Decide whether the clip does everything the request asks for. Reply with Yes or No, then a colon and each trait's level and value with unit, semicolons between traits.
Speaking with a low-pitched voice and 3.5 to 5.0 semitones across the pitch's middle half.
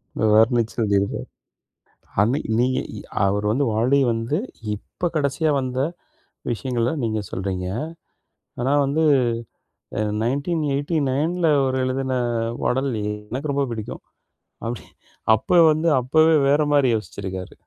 Yes: low, 130 Hz; average, 4.3 semitones